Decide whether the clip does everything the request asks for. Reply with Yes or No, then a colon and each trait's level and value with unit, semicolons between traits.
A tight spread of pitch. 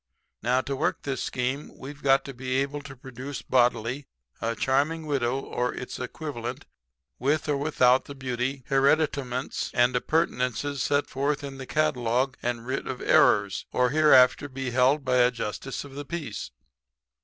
Yes: narrow, 2.2 semitones